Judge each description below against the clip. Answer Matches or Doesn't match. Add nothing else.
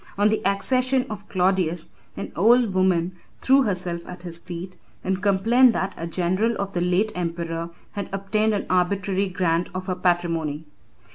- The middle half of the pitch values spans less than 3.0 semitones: Matches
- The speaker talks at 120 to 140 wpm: Doesn't match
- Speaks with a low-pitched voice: Doesn't match